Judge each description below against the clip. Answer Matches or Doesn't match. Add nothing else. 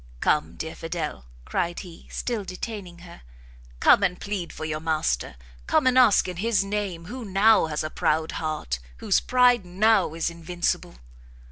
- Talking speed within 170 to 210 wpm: Doesn't match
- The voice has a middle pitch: Matches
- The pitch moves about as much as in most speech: Matches